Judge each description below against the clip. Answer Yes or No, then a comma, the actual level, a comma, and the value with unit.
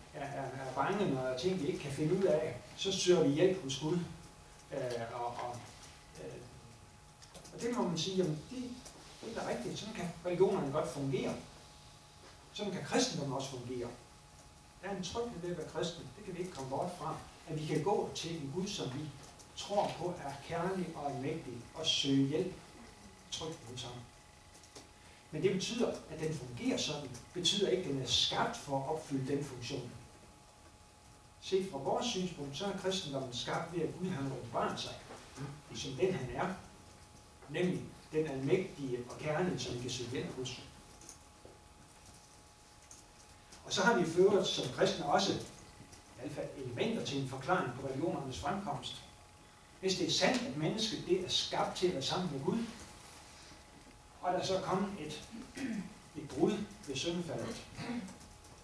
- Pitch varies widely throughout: Yes, wide, 6.0 semitones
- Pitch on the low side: No, medium, 155 Hz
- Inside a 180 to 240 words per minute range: No, average, 170 wpm